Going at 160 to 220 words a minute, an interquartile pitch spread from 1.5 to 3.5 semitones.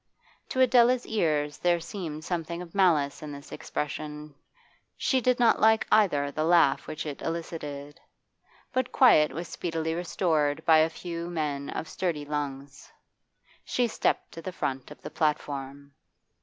No: average, 150 wpm; average, 3.2 semitones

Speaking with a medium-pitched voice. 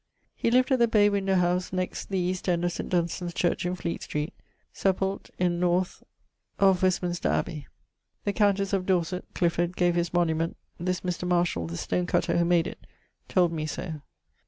Yes: medium, 180 Hz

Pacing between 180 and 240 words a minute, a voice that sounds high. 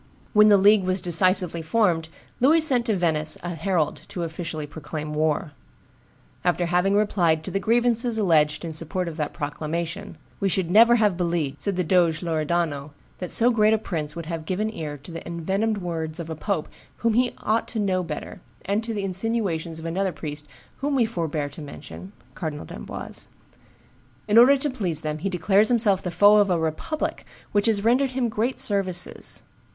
No: average, 185 wpm; medium, 180 Hz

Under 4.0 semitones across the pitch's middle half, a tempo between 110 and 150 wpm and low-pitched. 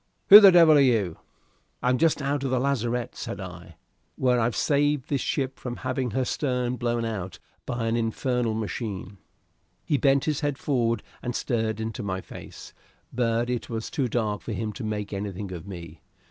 No: average, 3.5 semitones; average, 185 wpm; low, 120 Hz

